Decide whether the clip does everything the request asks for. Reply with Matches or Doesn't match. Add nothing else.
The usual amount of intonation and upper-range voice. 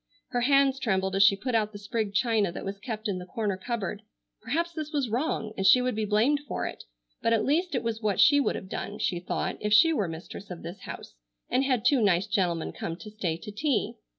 Matches